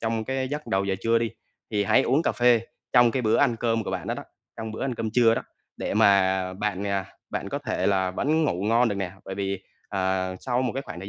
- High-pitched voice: No, low, 110 Hz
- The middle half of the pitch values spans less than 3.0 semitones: No, average, 3.9 semitones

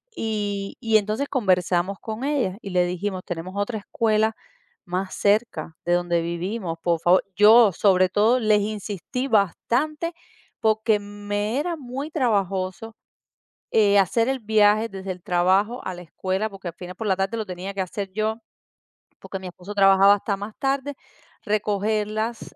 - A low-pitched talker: No, high, 205 Hz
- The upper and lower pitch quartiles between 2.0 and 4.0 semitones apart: Yes, average, 2.8 semitones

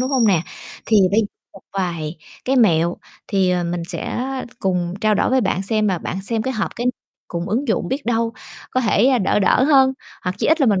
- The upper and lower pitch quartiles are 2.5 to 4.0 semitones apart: No, average, 5.2 semitones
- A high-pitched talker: Yes, high, 210 Hz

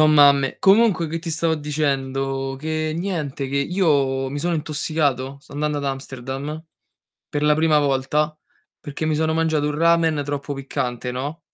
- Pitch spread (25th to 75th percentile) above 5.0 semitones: No, narrow, 2.6 semitones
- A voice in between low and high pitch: Yes, medium, 150 Hz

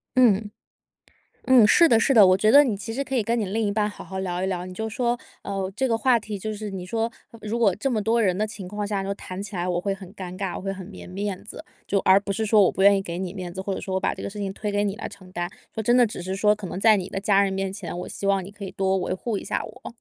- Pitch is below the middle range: No, high, 200 Hz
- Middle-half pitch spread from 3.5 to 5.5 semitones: No, narrow, 2.4 semitones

